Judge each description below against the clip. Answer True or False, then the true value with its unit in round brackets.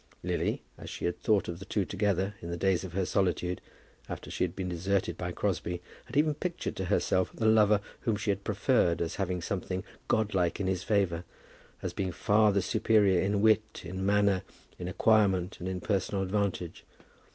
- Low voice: True (95 Hz)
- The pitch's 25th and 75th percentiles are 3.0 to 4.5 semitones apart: False (2.5 semitones)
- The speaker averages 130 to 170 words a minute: False (190 wpm)